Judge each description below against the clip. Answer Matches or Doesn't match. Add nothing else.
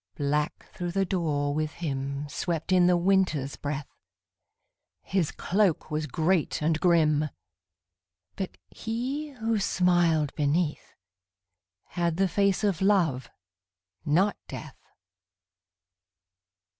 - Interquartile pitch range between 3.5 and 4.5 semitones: Matches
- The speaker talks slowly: Matches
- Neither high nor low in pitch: Matches